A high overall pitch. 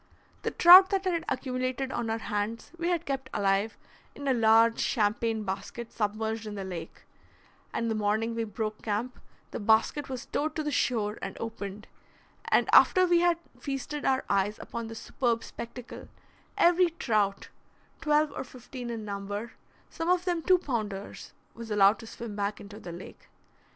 Yes: high, 230 Hz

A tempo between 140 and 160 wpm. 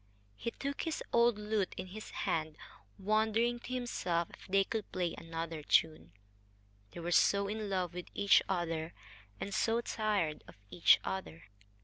Yes: average, 155 wpm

